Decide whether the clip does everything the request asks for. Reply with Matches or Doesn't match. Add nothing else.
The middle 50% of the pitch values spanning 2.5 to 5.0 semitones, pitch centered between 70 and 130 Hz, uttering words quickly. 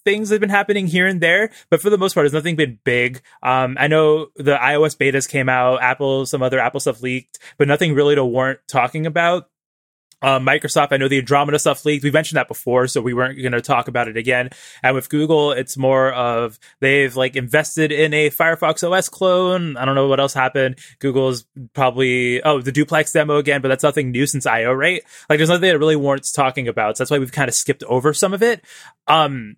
Doesn't match